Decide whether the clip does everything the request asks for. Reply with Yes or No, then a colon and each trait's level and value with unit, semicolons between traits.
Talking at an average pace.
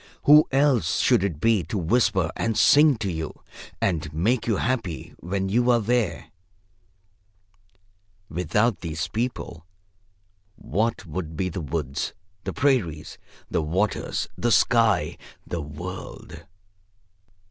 No: slow, 120 wpm